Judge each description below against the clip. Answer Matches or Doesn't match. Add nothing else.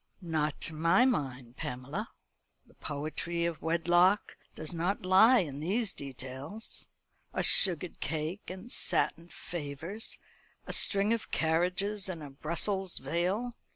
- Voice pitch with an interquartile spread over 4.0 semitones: Matches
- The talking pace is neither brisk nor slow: Doesn't match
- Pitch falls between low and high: Matches